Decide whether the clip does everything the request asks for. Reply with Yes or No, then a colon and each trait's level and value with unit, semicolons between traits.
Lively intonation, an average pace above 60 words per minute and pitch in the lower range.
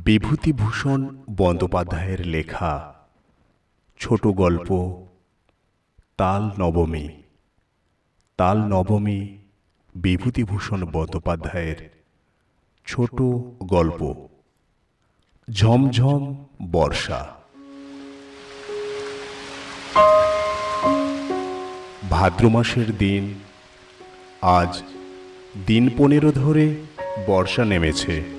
No: wide, 5.9 semitones; average, 50 wpm; low, 100 Hz